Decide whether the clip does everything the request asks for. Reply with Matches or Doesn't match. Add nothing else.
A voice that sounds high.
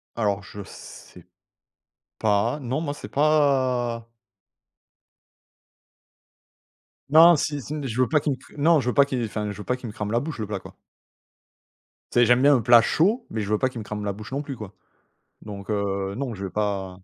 Doesn't match